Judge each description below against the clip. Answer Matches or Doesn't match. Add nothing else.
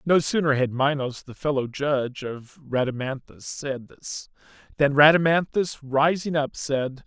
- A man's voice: Matches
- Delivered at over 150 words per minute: Doesn't match